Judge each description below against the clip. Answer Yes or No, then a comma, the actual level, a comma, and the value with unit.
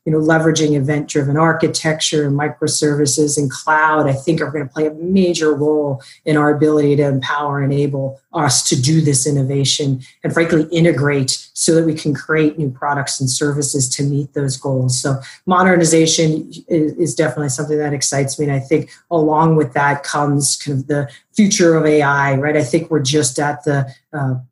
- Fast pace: No, average, 185 wpm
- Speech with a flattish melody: Yes, narrow, 1.8 semitones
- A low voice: No, medium, 150 Hz